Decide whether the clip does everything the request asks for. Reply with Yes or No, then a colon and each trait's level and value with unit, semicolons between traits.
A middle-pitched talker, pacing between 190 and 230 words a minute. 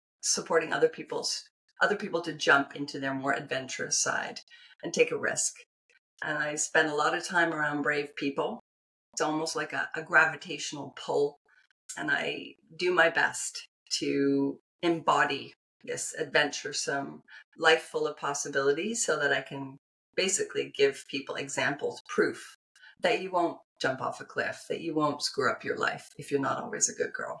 No: medium, 160 Hz; average, 165 wpm